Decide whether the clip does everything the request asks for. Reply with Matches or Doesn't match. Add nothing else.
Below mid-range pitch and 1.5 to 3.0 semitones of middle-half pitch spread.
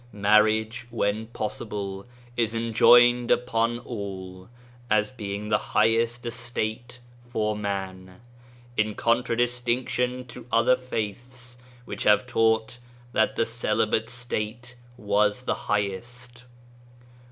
Matches